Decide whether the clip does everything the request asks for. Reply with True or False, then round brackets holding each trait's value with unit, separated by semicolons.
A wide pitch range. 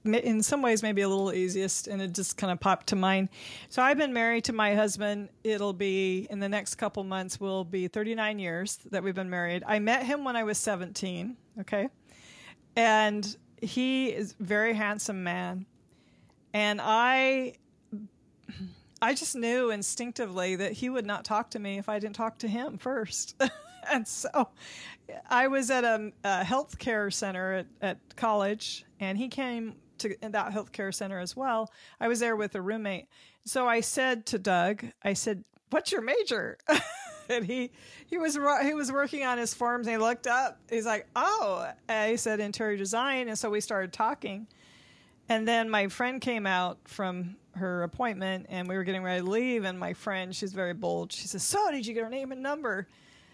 False (3.8 semitones)